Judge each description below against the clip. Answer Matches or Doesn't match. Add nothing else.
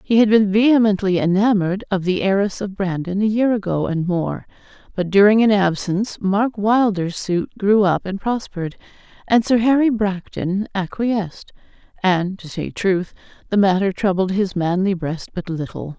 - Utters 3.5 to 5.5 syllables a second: Matches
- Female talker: Matches